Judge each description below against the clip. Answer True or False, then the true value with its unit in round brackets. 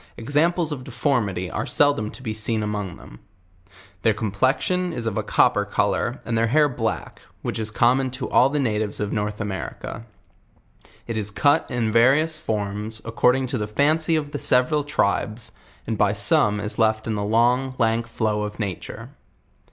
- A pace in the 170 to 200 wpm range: True (175 wpm)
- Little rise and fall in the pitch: False (4.1 semitones)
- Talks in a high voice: False (115 Hz)